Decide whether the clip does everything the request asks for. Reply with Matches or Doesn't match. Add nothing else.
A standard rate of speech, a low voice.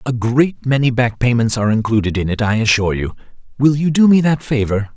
Doesn't match